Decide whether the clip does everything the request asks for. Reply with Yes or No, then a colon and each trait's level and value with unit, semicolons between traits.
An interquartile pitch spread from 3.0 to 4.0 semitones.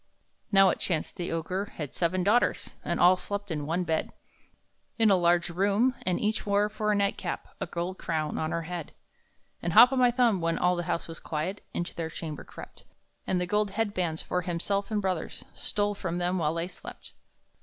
Yes: average, 3.3 semitones